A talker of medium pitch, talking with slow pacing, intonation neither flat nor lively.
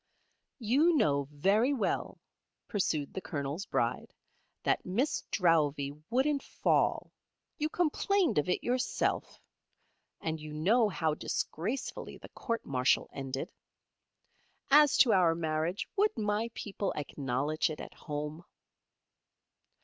No: medium, 180 Hz; slow, 115 wpm; wide, 8.3 semitones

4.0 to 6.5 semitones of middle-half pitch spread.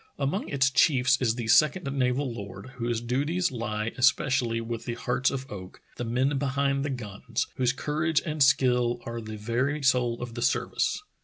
No: average, 2.7 semitones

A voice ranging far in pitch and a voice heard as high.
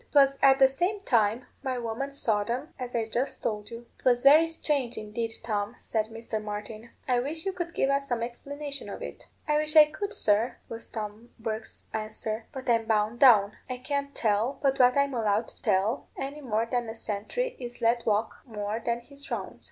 No: average, 4.1 semitones; high, 240 Hz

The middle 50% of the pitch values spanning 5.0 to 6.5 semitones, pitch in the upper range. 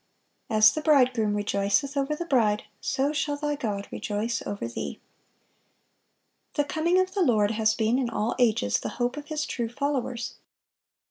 Yes: average, 5.3 semitones; high, 245 Hz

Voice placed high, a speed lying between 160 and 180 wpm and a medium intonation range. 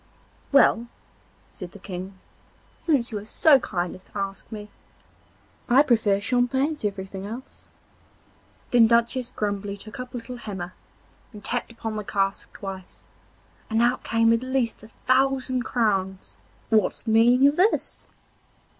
No: high, 225 Hz; average, 145 wpm; average, 3.9 semitones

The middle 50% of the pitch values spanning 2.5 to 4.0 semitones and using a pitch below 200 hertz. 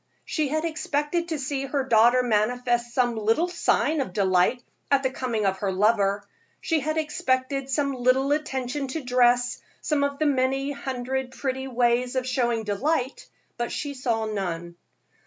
No: average, 2.9 semitones; very high, 255 Hz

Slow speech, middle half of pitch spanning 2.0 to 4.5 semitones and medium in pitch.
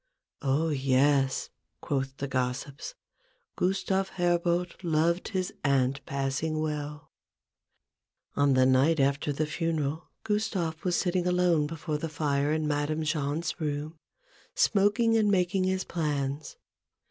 Yes: slow, 130 wpm; average, 4.0 semitones; medium, 155 Hz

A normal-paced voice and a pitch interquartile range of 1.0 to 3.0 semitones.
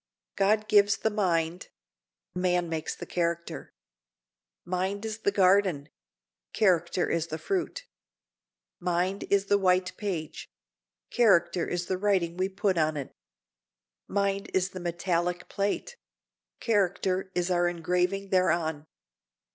No: slow, 120 wpm; narrow, 2.4 semitones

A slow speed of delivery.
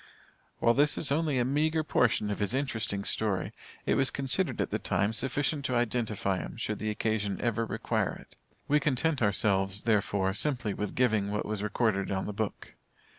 No: average, 180 wpm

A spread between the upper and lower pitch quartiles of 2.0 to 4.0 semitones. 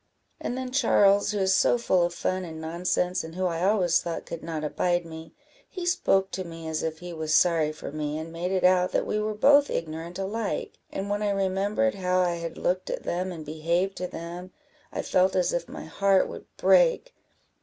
Yes: average, 2.9 semitones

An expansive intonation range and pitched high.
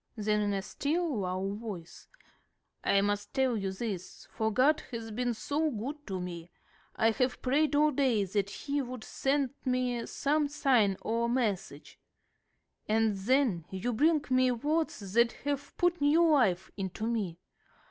Yes: wide, 5.7 semitones; high, 235 Hz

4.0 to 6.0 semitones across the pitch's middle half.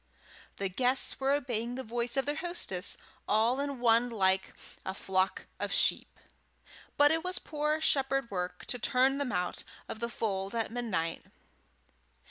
Yes: wide, 5.5 semitones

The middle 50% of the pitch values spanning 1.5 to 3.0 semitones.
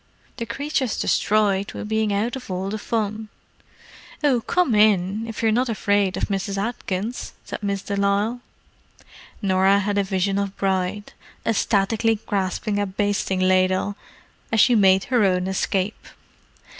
Yes: narrow, 2.4 semitones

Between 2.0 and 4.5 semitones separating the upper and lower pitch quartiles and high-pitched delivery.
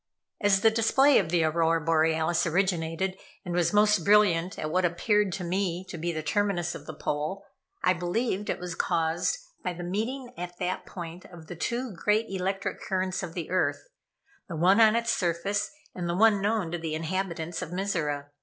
No: average, 3.4 semitones; medium, 180 Hz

